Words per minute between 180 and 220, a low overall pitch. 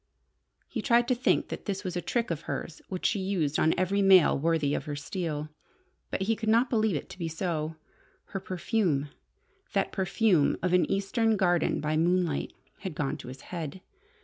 No: average, 190 wpm; medium, 180 Hz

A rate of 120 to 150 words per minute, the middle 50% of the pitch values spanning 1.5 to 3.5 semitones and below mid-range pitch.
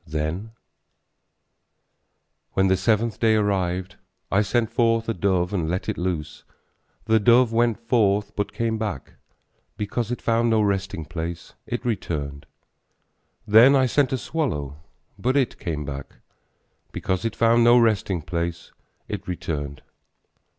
No: average, 140 wpm; average, 5.0 semitones; low, 105 Hz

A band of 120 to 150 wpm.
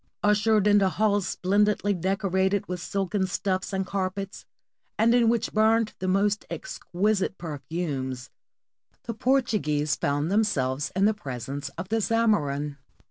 Yes: slow, 135 wpm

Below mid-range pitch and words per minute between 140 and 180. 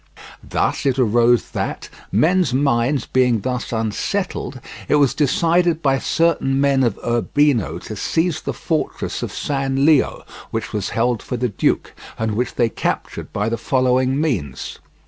Yes: low, 130 Hz; average, 150 wpm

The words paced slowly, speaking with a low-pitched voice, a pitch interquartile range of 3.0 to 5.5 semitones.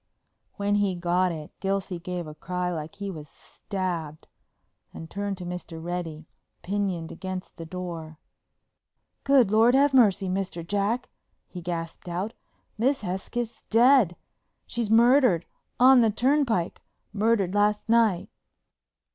No: slow, 120 wpm; high, 190 Hz; average, 4.3 semitones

